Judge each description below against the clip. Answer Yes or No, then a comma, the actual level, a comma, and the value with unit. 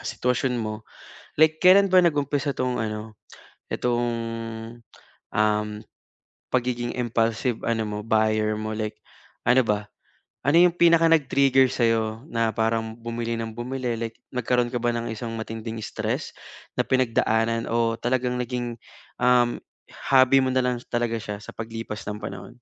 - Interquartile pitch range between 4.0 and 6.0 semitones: No, narrow, 2.4 semitones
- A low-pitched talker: Yes, low, 120 Hz